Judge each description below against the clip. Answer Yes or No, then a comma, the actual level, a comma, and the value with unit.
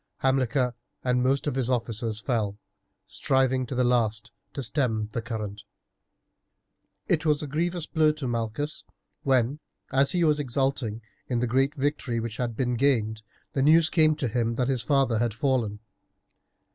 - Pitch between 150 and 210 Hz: No, low, 125 Hz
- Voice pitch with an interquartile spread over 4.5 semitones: No, average, 3.4 semitones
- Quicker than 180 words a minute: No, average, 160 wpm